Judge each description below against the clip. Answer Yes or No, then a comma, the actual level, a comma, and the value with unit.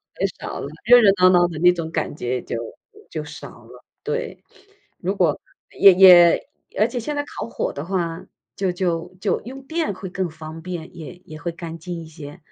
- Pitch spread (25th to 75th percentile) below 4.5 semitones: Yes, average, 3.1 semitones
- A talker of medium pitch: Yes, medium, 175 Hz